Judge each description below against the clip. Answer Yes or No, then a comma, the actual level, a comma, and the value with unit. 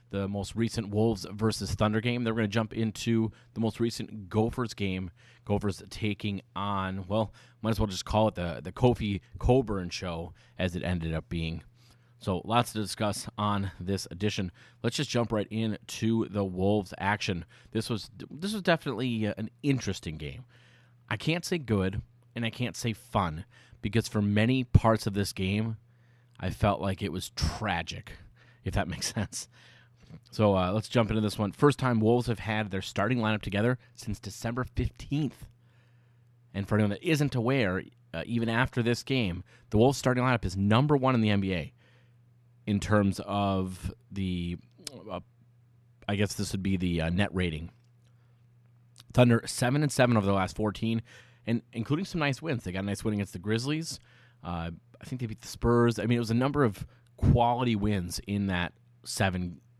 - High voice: No, low, 110 Hz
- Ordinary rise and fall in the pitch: Yes, average, 3.3 semitones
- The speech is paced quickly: No, average, 180 wpm